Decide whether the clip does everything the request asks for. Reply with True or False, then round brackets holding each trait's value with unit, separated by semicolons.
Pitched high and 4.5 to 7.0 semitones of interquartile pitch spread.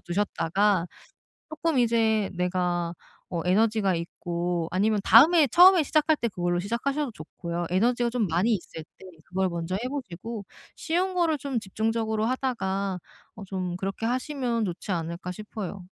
True (210 Hz; 5.4 semitones)